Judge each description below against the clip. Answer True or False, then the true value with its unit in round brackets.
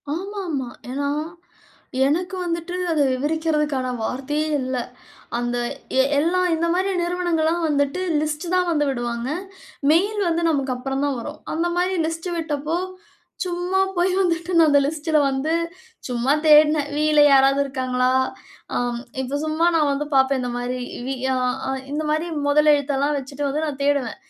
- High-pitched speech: True (300 Hz)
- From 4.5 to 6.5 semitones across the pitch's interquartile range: False (3.6 semitones)